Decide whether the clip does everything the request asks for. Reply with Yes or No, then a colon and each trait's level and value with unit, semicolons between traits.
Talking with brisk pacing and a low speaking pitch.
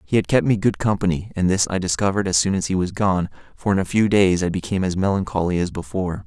Yes: fast, 260 wpm; very low, 95 Hz